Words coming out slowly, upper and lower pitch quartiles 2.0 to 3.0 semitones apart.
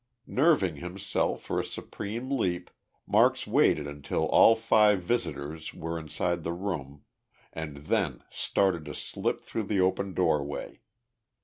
No: slow, 130 wpm; average, 5.0 semitones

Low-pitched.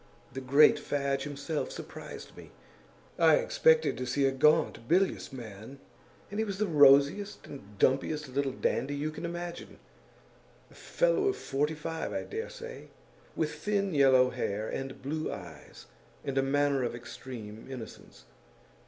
No: medium, 145 Hz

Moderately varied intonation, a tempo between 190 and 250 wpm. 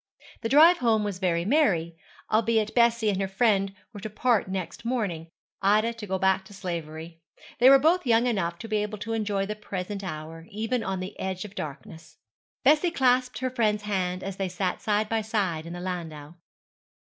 Yes: average, 3.9 semitones; average, 195 wpm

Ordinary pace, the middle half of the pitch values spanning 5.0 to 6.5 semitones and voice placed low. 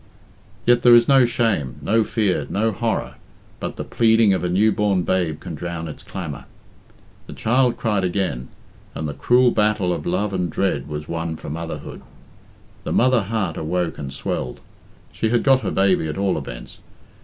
Yes: average, 180 wpm; wide, 5.5 semitones; very low, 95 Hz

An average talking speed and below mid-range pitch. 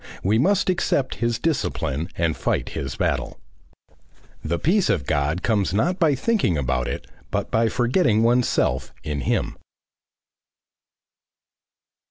No: slow, 125 wpm; low, 110 Hz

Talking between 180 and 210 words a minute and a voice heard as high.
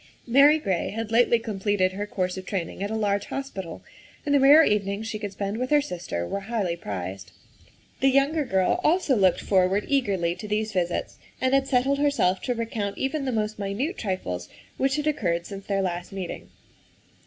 Yes: average, 190 wpm; high, 210 Hz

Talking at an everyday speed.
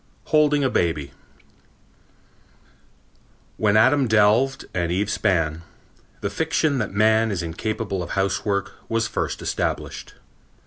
No: slow, 115 wpm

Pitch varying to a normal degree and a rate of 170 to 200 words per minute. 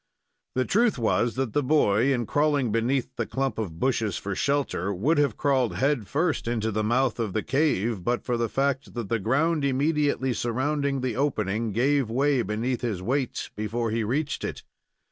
Yes: average, 4.0 semitones; average, 185 wpm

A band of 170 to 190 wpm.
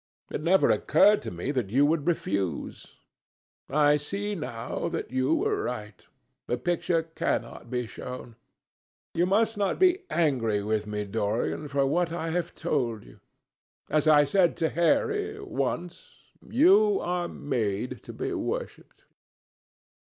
No: average, 140 wpm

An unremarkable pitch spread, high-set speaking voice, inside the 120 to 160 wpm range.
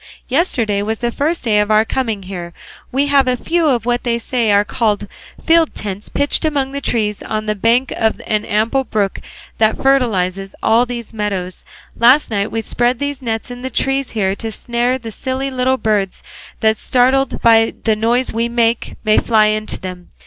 No: average, 3.4 semitones; high, 230 Hz; average, 190 wpm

